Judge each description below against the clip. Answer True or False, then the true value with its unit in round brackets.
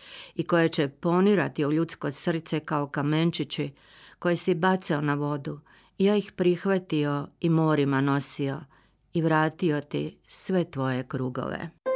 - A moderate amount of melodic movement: True (3.4 semitones)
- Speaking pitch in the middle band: True (155 Hz)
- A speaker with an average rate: True (135 wpm)